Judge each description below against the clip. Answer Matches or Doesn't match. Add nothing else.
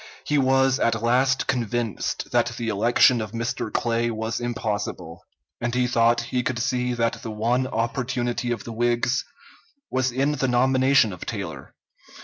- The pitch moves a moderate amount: Doesn't match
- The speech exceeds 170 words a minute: Doesn't match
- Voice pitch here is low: Matches